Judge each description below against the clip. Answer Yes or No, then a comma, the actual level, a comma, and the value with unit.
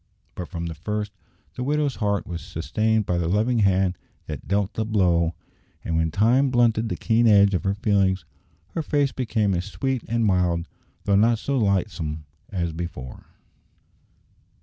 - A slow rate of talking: No, average, 165 wpm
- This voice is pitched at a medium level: No, low, 100 Hz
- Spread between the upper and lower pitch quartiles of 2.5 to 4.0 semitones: No, average, 4.4 semitones